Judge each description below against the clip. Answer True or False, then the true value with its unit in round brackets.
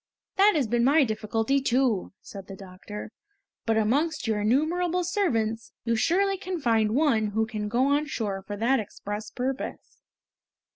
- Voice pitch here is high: True (235 Hz)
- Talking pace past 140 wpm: True (155 wpm)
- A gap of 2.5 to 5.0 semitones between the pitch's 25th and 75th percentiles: False (5.5 semitones)